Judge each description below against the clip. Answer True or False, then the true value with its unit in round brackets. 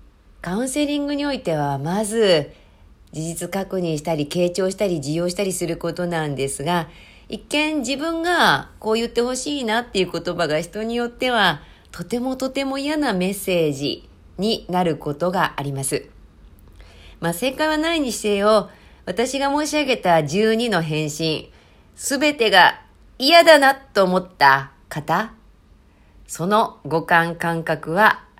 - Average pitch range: False (6.9 semitones)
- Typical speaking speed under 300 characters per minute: True (275 characters per minute)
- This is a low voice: False (185 Hz)